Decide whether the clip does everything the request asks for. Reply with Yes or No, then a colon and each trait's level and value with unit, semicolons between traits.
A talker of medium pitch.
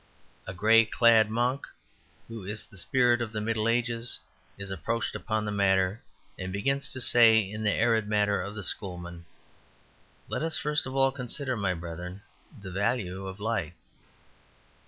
No: low, 110 Hz